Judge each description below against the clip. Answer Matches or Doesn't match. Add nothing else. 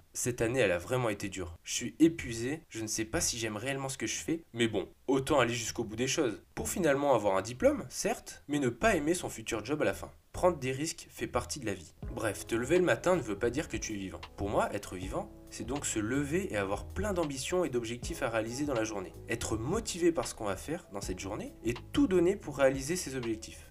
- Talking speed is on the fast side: Matches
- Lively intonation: Matches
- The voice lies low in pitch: Matches